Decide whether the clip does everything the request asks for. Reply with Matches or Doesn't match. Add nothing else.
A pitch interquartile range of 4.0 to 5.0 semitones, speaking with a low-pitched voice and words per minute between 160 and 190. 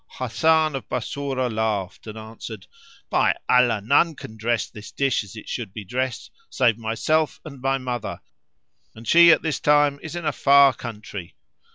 Matches